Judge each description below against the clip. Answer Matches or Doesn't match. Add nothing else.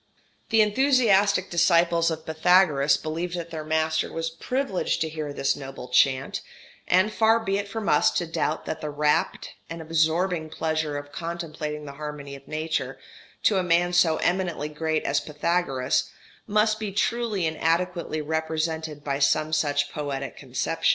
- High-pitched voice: Doesn't match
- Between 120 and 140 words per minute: Doesn't match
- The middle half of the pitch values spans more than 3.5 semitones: Doesn't match